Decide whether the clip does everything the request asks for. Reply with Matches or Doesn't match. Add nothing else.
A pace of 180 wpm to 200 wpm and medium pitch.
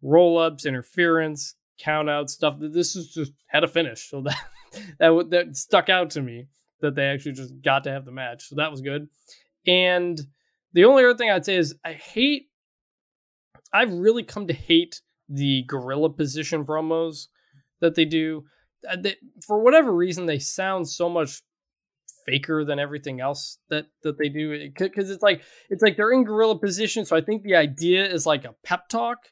Matches